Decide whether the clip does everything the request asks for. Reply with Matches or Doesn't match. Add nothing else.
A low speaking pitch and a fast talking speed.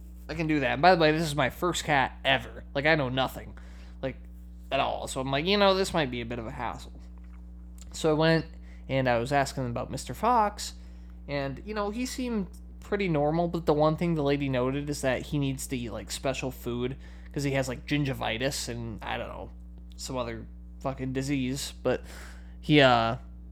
Matches